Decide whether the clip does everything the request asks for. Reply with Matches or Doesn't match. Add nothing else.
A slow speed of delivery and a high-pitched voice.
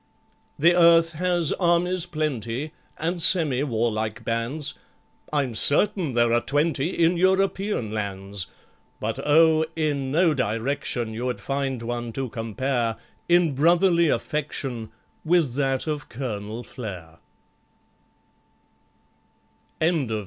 Doesn't match